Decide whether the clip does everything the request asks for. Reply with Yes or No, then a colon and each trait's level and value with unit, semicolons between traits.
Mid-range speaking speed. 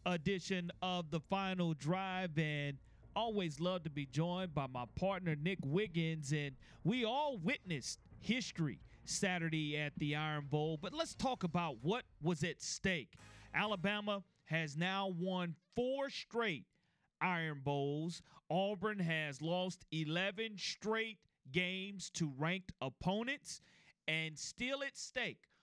No: slow, 130 wpm